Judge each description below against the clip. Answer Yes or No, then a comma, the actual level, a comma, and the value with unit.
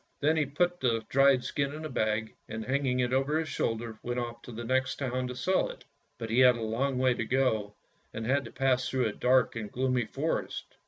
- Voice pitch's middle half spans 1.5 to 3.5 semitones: Yes, average, 2.7 semitones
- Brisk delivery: Yes, fast, 230 wpm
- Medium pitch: No, low, 125 Hz